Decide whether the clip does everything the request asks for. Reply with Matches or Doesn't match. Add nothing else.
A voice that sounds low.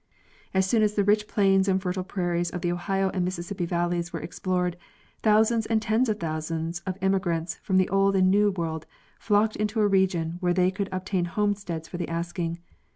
Doesn't match